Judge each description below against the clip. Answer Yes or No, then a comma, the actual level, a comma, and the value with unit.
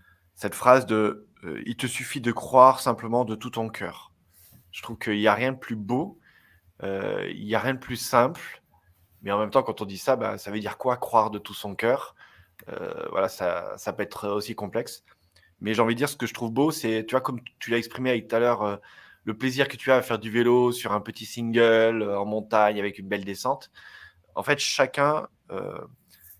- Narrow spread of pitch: No, average, 3.0 semitones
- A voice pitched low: Yes, low, 115 Hz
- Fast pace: Yes, fast, 230 wpm